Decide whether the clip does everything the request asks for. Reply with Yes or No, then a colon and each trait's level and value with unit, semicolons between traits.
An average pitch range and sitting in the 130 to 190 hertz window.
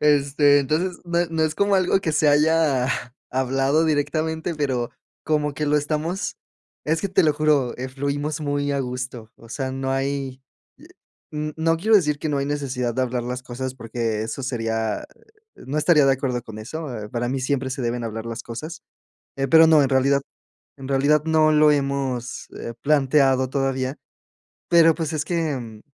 Yes: average, 3.1 semitones; medium, 140 Hz